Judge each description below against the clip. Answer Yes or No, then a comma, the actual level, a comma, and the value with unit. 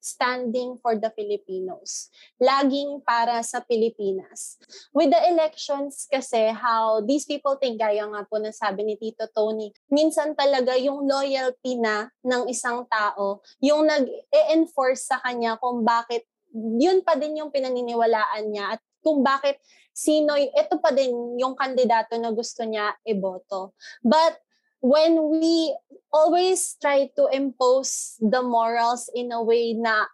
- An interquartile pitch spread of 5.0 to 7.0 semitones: No, average, 4.3 semitones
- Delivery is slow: No, average, 140 wpm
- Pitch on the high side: Yes, very high, 255 Hz